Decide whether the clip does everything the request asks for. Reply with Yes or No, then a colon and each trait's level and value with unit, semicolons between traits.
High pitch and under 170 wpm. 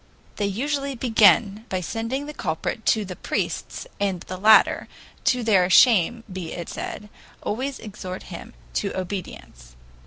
Yes: high, 205 Hz; average, 145 wpm